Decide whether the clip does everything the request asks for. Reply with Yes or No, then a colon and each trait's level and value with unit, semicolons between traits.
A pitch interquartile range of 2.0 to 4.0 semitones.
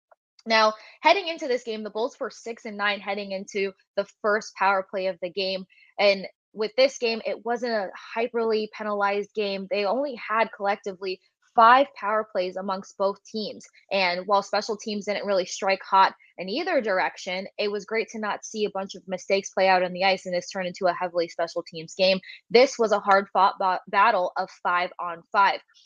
Yes: narrow, 2.4 semitones